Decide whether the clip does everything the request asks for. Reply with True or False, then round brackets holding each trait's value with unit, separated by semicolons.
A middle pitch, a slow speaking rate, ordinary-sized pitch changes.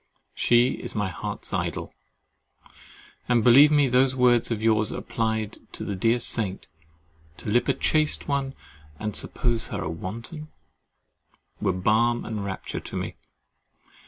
False (115 Hz; 130 wpm; 4.1 semitones)